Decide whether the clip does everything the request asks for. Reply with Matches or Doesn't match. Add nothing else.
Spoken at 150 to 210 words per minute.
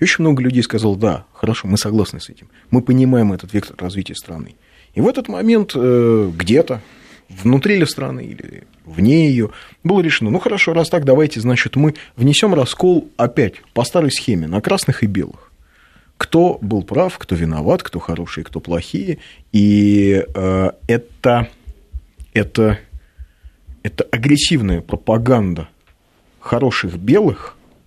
Doesn't match